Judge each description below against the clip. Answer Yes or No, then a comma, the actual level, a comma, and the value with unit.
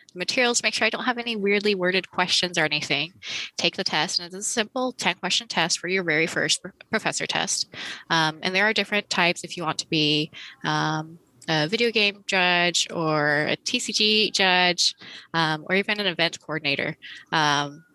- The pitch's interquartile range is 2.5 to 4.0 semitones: No, average, 4.7 semitones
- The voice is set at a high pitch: No, medium, 180 Hz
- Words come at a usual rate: Yes, average, 185 wpm